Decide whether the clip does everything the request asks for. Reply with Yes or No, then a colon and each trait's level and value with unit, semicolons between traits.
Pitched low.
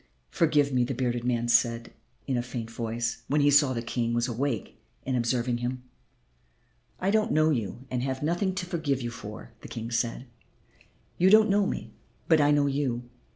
Yes: low, 125 Hz